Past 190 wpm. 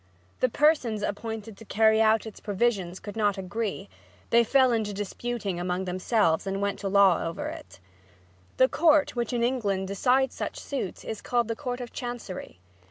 No: average, 170 wpm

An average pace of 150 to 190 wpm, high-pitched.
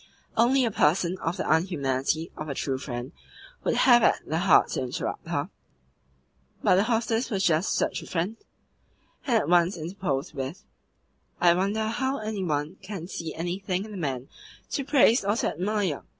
No: average, 175 wpm; medium, 180 Hz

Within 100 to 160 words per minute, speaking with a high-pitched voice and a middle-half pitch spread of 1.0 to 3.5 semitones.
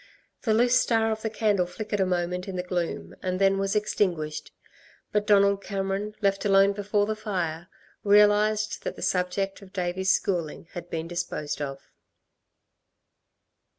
Yes: average, 150 wpm; high, 195 Hz; average, 2.7 semitones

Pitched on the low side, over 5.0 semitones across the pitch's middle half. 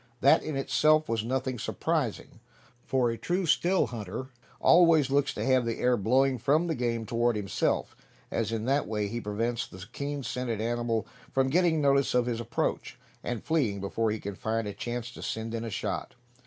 No: low, 120 Hz; average, 3.5 semitones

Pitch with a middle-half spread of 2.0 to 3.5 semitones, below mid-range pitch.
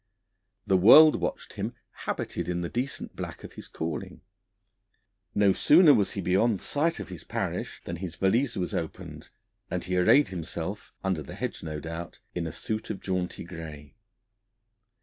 No: average, 4.5 semitones; very low, 90 Hz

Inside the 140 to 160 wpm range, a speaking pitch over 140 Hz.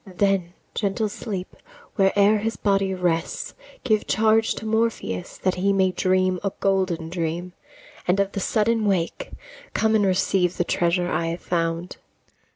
Yes: average, 150 wpm; high, 190 Hz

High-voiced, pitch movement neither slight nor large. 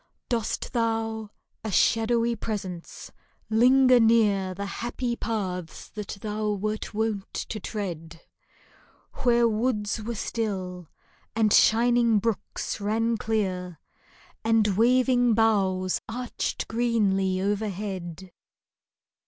Yes: high, 215 Hz; average, 3.0 semitones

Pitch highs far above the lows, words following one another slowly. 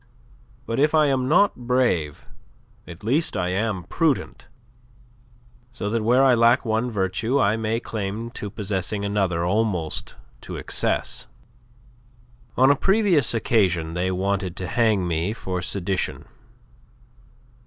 No: average, 4.8 semitones; slow, 130 wpm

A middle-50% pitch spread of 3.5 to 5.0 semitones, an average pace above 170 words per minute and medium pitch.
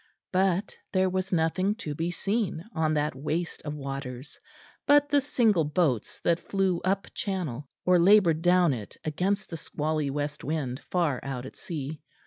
No: average, 4.2 semitones; average, 160 wpm; medium, 165 Hz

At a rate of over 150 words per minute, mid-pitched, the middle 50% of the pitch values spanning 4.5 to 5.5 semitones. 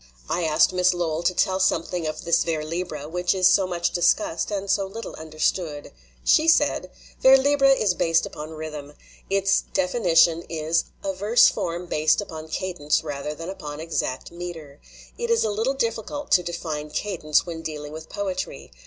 No: average, 175 wpm; medium, 170 Hz; average, 3.7 semitones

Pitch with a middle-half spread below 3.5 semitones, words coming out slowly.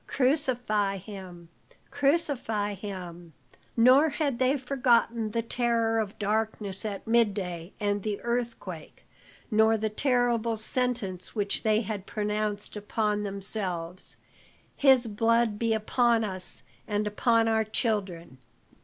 Yes: average, 2.8 semitones; slow, 115 wpm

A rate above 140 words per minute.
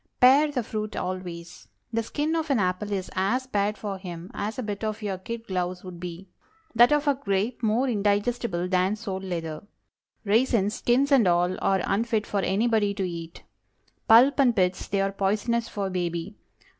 Yes: average, 170 wpm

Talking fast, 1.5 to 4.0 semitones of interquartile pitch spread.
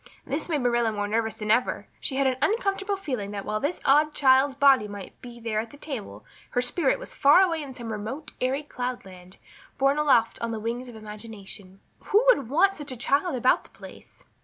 No: fast, 210 wpm; average, 4.8 semitones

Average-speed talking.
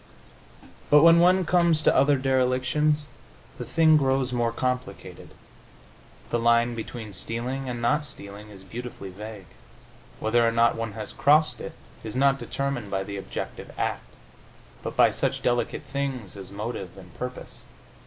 Yes: average, 150 wpm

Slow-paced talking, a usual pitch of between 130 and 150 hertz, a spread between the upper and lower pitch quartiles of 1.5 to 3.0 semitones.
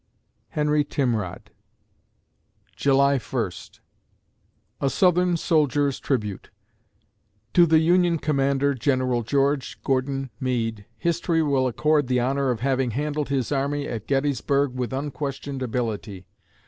Yes: slow, 110 wpm; low, 135 Hz; average, 2.7 semitones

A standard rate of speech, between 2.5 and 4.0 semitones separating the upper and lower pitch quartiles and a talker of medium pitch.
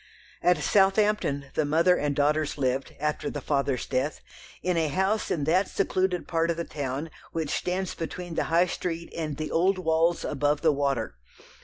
Yes: average, 175 wpm; average, 3.7 semitones; medium, 160 Hz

